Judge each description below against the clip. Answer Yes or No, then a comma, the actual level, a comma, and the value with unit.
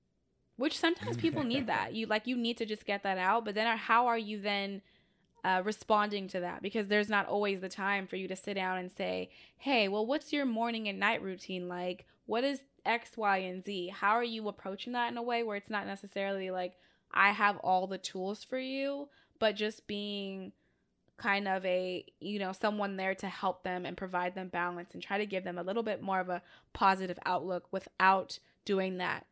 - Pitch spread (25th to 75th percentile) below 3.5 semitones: Yes, average, 3.0 semitones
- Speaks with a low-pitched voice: No, high, 200 Hz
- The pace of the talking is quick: Yes, fast, 215 wpm